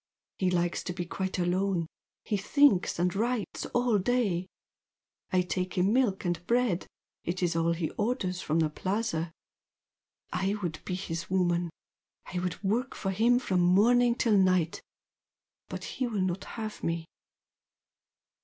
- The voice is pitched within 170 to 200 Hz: Yes, medium, 185 Hz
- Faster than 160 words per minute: No, average, 150 wpm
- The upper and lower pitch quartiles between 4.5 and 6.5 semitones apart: No, average, 3.8 semitones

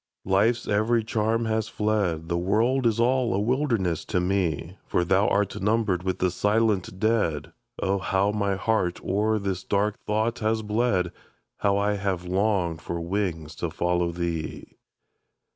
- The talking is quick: No, average, 155 wpm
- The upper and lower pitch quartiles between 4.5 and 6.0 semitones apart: No, average, 3.6 semitones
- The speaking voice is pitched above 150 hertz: No, low, 100 Hz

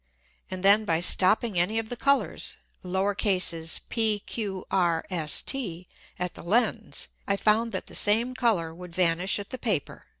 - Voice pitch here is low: No, high, 200 Hz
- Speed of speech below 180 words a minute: Yes, average, 160 wpm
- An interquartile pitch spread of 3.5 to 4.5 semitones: Yes, average, 4.1 semitones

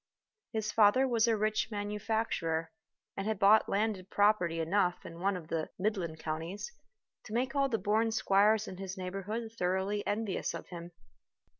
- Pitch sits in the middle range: No, high, 205 Hz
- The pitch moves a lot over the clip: No, average, 3.2 semitones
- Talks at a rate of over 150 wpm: Yes, average, 160 wpm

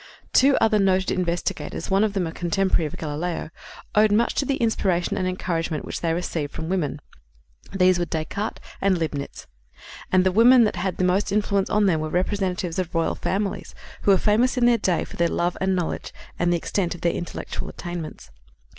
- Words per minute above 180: Yes, average, 195 wpm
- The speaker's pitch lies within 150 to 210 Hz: Yes, medium, 185 Hz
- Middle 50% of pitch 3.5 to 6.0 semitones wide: No, average, 2.9 semitones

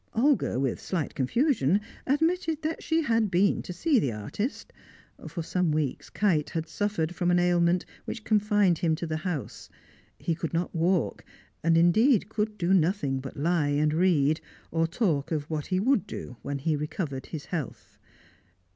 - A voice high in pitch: No, medium, 175 Hz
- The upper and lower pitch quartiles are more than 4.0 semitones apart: Yes, average, 5.3 semitones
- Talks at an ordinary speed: Yes, average, 170 wpm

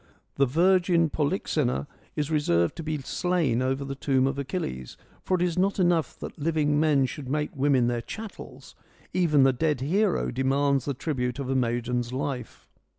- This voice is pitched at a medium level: Yes, medium, 145 Hz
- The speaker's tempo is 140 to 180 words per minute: Yes, average, 170 wpm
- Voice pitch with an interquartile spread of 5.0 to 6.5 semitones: No, average, 4.0 semitones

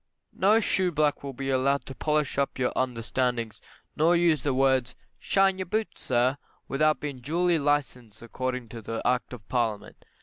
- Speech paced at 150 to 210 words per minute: Yes, average, 160 wpm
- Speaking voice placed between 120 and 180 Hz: Yes, low, 135 Hz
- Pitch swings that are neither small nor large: Yes, average, 3.7 semitones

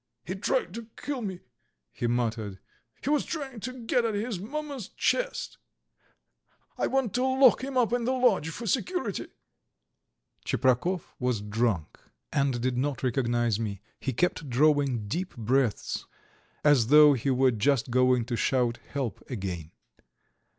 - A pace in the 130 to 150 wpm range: Yes, average, 145 wpm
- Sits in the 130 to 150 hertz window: Yes, medium, 140 Hz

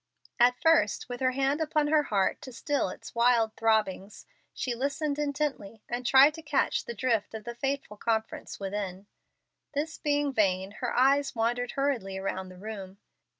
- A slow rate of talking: No, average, 165 wpm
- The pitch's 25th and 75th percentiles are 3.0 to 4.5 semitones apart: No, average, 5.1 semitones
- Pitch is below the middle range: No, high, 240 Hz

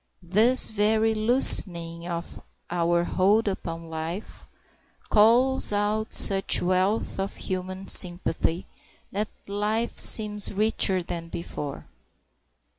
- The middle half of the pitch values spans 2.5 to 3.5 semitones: No, average, 3.9 semitones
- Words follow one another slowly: Yes, slow, 100 wpm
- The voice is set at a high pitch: Yes, high, 195 Hz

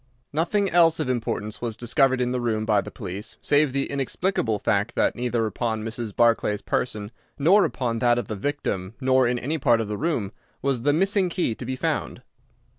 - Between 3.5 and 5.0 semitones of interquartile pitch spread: Yes, average, 4.5 semitones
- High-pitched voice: No, low, 120 Hz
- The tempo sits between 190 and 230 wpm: Yes, average, 195 wpm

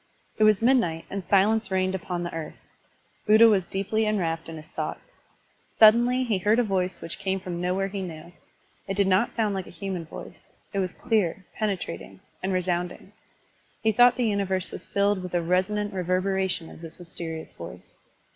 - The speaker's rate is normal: Yes, average, 180 wpm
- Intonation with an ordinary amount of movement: Yes, average, 3.0 semitones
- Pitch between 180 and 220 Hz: Yes, high, 190 Hz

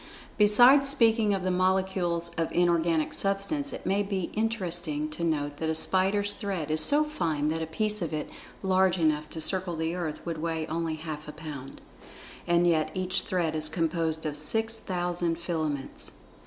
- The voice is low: No, medium, 170 Hz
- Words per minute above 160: Yes, average, 175 wpm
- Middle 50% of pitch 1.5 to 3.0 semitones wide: No, average, 3.4 semitones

